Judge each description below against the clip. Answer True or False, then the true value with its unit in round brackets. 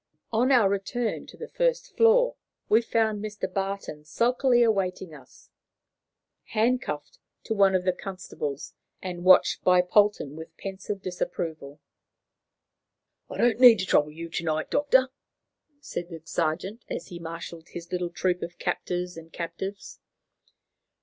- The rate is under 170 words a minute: True (135 wpm)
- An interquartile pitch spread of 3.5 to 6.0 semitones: True (4.8 semitones)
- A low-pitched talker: False (185 Hz)